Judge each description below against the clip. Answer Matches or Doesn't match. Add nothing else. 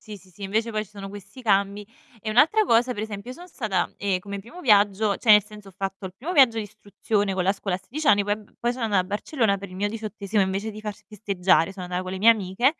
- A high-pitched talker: Matches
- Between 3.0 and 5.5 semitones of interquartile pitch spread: Doesn't match